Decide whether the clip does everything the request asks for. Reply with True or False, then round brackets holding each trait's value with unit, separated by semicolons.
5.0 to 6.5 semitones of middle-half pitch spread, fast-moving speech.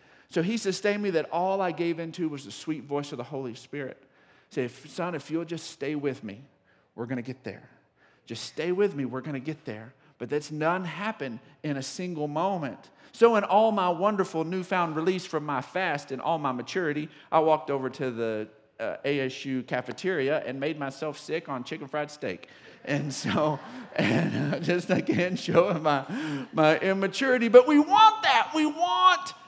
False (5.3 semitones; 190 wpm)